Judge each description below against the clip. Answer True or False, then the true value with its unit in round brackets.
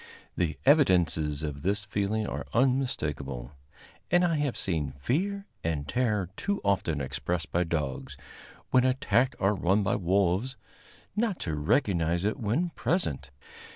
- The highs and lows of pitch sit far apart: True (8.5 semitones)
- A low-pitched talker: True (100 Hz)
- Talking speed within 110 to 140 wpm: True (135 wpm)